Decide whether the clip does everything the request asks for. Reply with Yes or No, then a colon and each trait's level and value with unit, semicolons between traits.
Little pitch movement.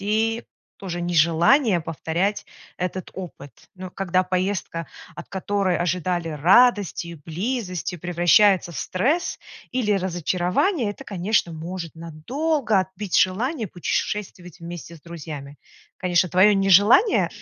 No: average, 3.4 semitones